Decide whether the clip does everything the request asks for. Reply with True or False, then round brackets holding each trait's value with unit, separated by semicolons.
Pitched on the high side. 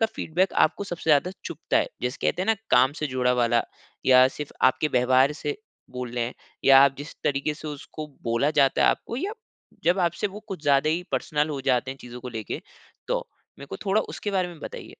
False (145 Hz)